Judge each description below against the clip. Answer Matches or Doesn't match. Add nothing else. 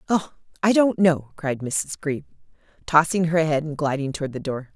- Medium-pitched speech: Matches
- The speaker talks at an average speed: Matches